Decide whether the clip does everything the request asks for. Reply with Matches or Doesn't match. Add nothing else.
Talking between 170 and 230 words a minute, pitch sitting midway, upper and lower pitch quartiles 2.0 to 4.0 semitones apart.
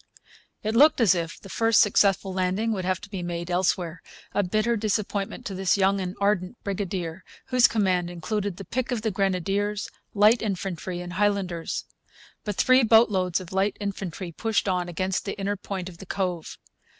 Doesn't match